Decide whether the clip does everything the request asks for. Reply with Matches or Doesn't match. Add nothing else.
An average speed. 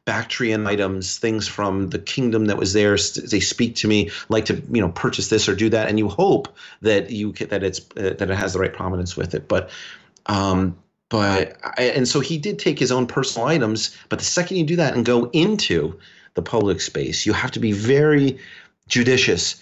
Doesn't match